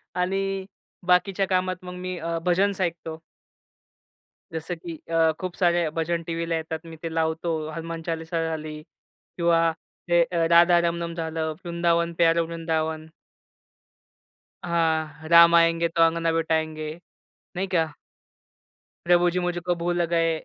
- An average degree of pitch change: No, narrow, 1.3 semitones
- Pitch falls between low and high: Yes, medium, 170 Hz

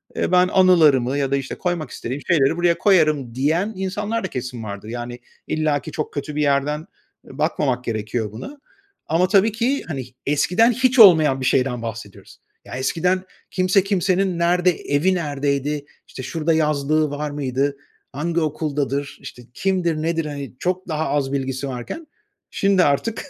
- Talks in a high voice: No, medium, 150 Hz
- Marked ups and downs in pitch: No, average, 5.0 semitones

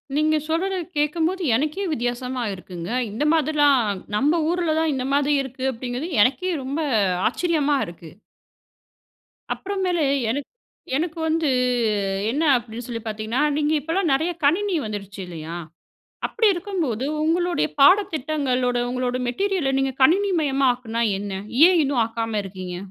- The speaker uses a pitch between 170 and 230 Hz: No, very high, 280 Hz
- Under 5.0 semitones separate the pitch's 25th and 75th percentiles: No, average, 5.3 semitones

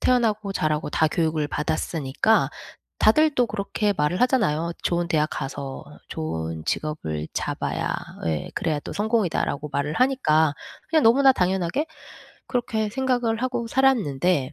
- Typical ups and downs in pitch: No, wide, 8.0 semitones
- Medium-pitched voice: Yes, medium, 180 Hz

